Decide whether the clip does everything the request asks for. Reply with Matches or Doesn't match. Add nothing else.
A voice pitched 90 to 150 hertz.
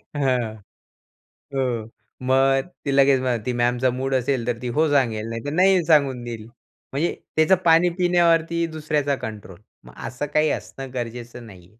Matches